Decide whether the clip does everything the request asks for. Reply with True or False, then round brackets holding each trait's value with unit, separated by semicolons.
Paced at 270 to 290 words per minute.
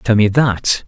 False (205 wpm)